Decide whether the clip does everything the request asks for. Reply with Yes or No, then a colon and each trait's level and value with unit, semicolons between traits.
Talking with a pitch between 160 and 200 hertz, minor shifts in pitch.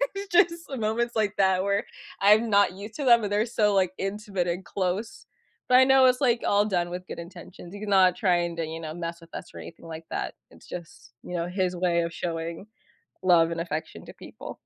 No: high, 190 Hz; average, 3.6 semitones